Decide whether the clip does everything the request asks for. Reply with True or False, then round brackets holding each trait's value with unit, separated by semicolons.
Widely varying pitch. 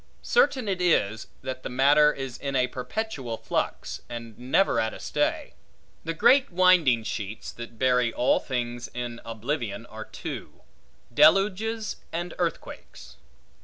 True (6.9 semitones)